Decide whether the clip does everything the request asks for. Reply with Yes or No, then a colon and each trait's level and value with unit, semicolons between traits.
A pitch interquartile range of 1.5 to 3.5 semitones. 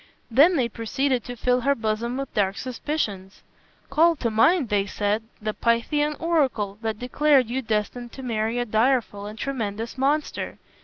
No: average, 4.1 semitones